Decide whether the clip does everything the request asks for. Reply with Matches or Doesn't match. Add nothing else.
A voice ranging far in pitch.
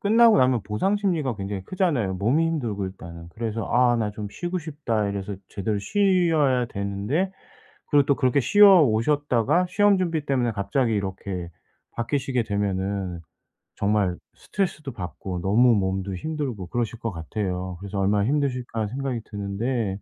Matches